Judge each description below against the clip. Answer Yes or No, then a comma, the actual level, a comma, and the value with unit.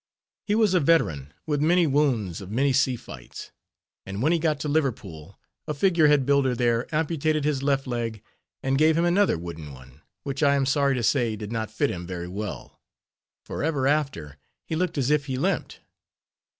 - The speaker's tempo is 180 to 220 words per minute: Yes, average, 190 wpm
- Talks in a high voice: No, low, 135 Hz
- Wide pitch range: Yes, wide, 6.0 semitones